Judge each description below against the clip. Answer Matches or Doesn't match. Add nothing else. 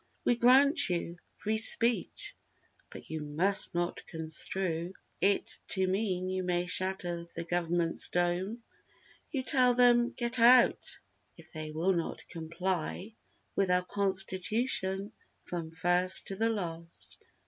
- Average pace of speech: Doesn't match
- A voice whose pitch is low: Doesn't match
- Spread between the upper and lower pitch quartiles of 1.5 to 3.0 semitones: Doesn't match